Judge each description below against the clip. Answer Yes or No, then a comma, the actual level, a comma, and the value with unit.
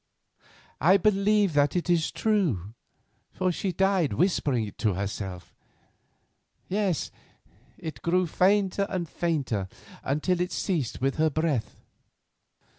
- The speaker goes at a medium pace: No, slow, 110 wpm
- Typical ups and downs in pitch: No, wide, 6.1 semitones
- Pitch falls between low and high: Yes, medium, 170 Hz